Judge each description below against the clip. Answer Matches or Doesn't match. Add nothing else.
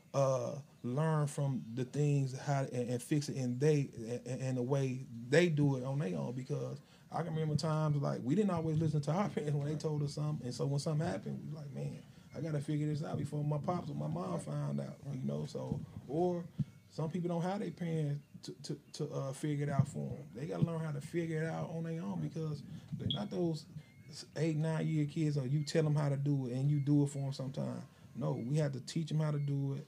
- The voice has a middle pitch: Matches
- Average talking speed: Doesn't match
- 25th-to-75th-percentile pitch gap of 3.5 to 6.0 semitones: Doesn't match